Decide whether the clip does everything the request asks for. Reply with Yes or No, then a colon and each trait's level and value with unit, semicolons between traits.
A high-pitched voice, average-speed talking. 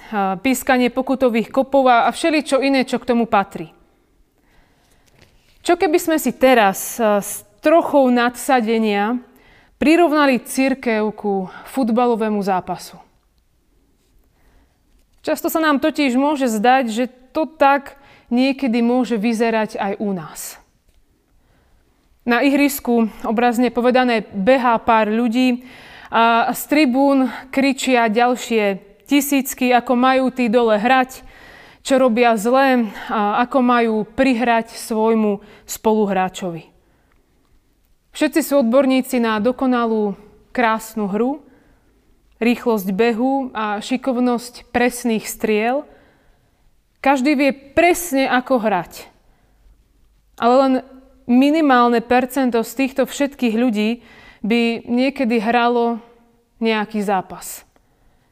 No: high, 245 Hz; slow, 100 wpm